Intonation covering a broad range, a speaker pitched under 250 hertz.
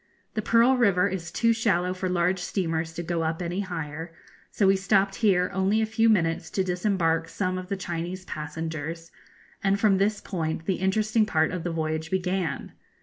No: average, 3.2 semitones; medium, 185 Hz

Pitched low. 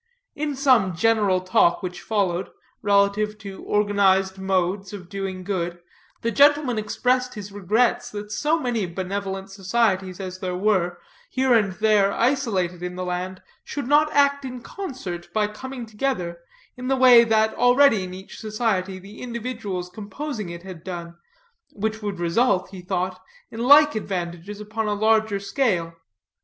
No: high, 205 Hz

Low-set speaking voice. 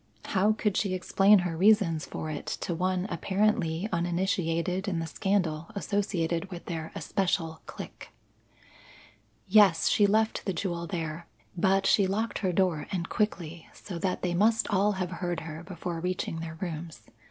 No: medium, 180 Hz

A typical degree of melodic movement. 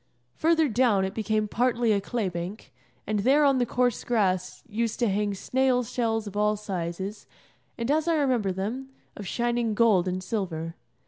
Yes: average, 4.0 semitones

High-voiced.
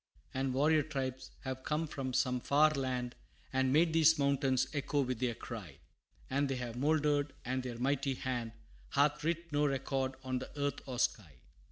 No: low, 135 Hz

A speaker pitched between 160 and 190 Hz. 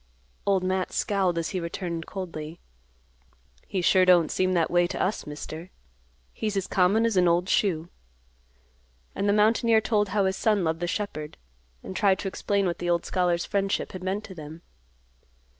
Yes: medium, 185 Hz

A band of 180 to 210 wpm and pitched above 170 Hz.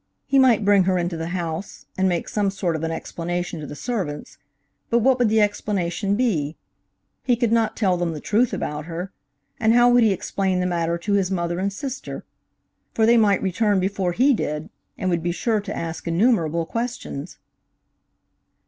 Yes: average, 190 wpm; high, 190 Hz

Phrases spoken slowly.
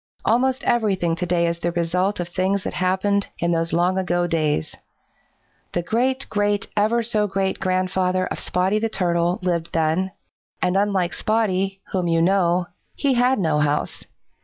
No: average, 160 wpm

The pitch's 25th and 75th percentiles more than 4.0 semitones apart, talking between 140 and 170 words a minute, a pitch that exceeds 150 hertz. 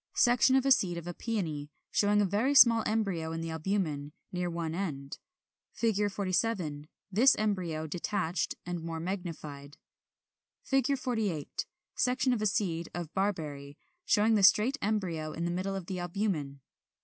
Yes: average, 4.8 semitones; average, 160 wpm; medium, 185 Hz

